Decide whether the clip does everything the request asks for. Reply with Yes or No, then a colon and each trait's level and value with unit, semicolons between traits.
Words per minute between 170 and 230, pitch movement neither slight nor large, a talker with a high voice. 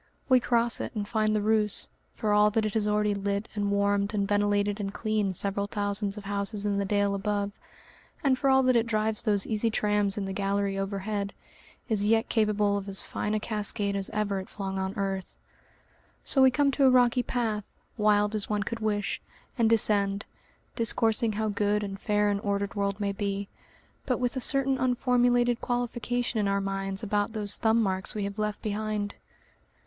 No: average, 195 wpm; narrow, 1.8 semitones; high, 210 Hz